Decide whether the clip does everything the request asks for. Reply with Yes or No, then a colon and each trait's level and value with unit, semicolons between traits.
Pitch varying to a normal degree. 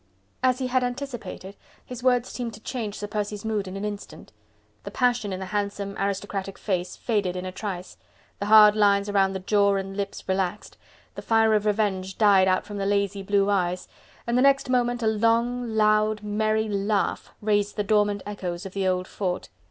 No: narrow, 2.0 semitones